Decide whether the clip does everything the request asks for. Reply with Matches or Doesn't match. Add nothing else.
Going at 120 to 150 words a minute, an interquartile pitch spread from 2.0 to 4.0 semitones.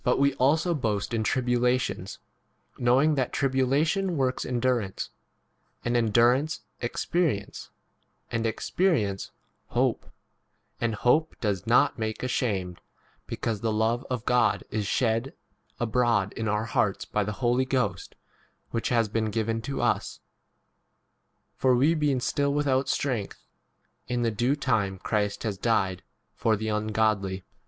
Matches